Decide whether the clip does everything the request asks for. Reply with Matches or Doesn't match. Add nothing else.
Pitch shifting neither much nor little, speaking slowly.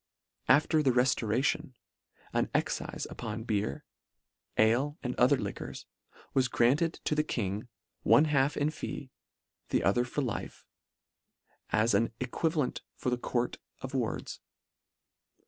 Matches